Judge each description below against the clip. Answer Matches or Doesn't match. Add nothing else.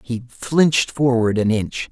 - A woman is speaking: Doesn't match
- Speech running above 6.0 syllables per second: Doesn't match